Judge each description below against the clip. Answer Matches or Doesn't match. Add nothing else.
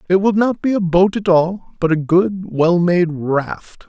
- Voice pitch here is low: Doesn't match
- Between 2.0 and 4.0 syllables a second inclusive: Matches